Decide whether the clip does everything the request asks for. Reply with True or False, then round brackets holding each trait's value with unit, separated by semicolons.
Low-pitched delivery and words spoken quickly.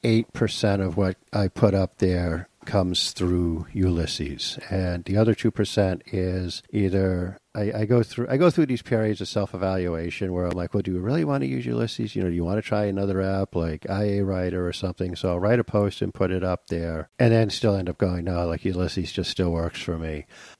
True (95 Hz; 230 wpm)